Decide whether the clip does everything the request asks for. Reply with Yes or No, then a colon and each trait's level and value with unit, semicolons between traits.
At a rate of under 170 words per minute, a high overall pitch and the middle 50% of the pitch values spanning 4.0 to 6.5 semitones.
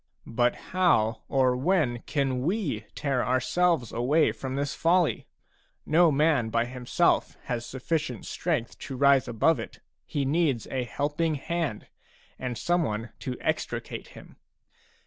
No: slow, 135 wpm; low, 135 Hz; average, 4.7 semitones